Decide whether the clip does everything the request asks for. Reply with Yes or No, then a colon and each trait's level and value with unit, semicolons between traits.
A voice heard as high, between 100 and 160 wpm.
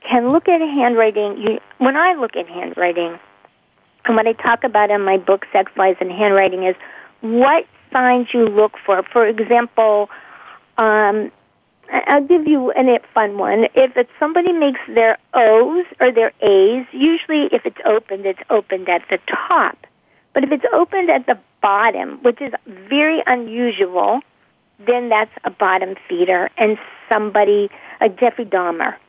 Yes: high, 225 Hz; average, 155 wpm